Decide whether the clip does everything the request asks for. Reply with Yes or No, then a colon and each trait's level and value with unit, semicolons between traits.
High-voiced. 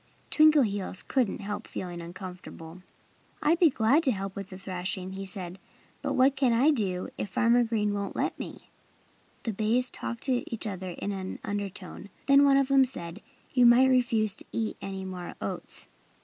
Yes: high, 210 Hz